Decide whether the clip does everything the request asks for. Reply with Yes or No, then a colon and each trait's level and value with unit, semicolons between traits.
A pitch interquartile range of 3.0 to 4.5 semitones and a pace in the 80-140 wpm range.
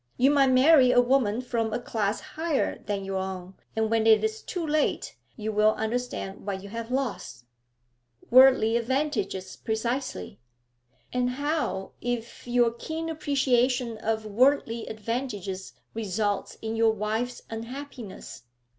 Yes: average, 3.5 semitones; slow, 135 wpm